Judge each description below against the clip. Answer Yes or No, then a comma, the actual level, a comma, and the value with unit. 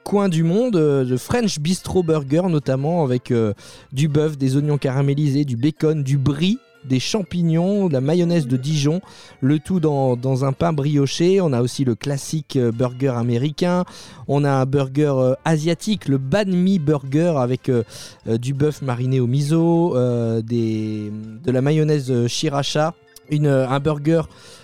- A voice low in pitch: No, medium, 145 Hz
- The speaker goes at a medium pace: Yes, average, 170 wpm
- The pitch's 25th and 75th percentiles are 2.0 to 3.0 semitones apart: No, average, 4.1 semitones